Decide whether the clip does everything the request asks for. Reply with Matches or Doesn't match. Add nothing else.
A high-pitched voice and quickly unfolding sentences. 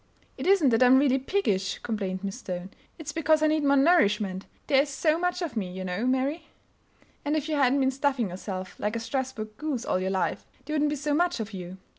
Matches